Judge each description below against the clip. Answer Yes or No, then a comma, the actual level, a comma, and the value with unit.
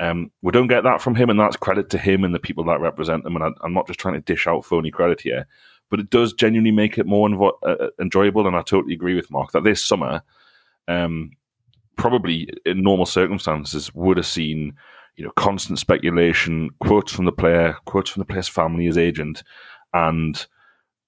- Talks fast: Yes, fast, 210 wpm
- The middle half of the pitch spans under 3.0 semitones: No, average, 4.1 semitones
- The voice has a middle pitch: No, very low, 90 Hz